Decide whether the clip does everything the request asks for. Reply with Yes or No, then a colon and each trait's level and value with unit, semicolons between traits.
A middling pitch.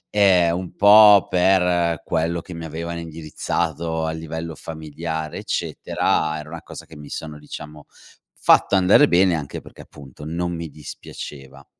No: very low, 80 Hz